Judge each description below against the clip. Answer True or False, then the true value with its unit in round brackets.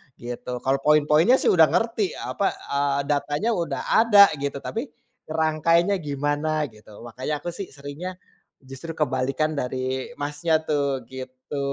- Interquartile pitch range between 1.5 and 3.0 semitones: False (3.5 semitones)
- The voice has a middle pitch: True (145 Hz)